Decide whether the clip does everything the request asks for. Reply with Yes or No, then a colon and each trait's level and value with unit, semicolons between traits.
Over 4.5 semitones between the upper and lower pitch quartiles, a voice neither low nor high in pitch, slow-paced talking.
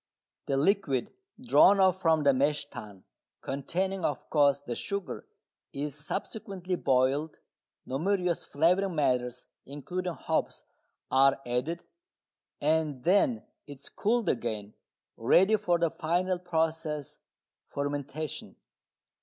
Yes: average, 4.9 semitones; medium, 155 Hz; slow, 110 wpm